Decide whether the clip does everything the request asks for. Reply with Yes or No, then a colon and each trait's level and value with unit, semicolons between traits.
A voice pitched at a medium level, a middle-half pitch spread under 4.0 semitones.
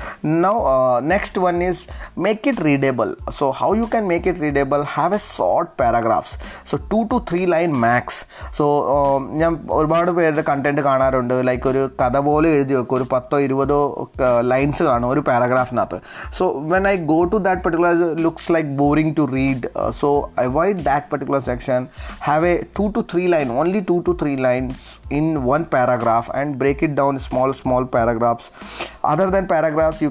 No: medium, 145 Hz; average, 4.5 semitones